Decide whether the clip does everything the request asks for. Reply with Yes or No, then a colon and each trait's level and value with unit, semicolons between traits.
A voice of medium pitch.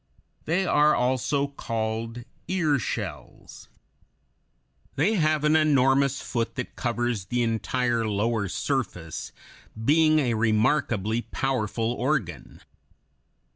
No: low, 125 Hz